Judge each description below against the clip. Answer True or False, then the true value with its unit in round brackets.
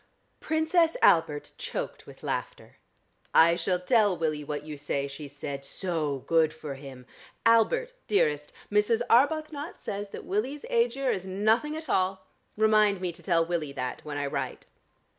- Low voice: False (185 Hz)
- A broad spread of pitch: True (7.6 semitones)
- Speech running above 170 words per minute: False (155 wpm)